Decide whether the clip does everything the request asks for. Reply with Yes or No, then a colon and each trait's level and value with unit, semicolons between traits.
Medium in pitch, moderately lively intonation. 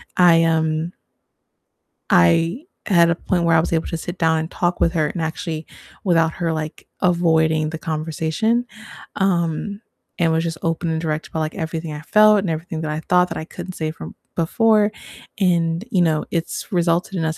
No: medium, 165 Hz; narrow, 1.8 semitones